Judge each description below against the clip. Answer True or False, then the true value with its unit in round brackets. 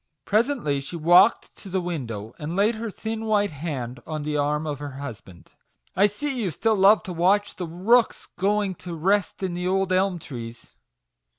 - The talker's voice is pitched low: False (180 Hz)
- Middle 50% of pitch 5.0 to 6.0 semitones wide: True (5.6 semitones)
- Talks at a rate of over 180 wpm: True (190 wpm)